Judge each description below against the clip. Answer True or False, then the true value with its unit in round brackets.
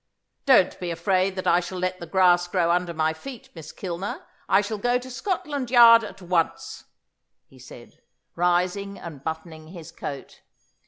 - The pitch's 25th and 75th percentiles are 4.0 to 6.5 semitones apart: False (3.4 semitones)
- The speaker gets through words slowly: False (165 wpm)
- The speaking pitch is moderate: True (180 Hz)